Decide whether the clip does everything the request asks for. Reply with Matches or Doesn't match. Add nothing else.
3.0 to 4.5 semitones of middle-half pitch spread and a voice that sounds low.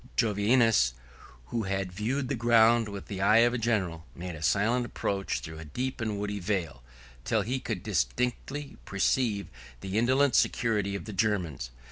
Matches